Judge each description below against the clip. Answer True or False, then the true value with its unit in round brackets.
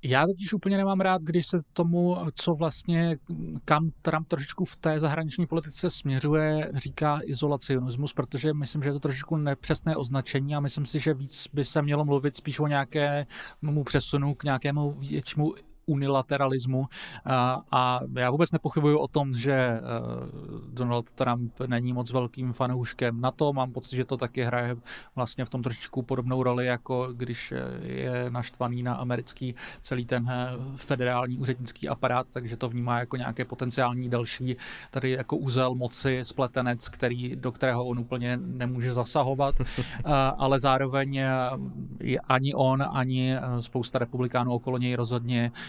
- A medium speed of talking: True (150 wpm)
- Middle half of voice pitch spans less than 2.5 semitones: False (2.8 semitones)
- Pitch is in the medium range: False (130 Hz)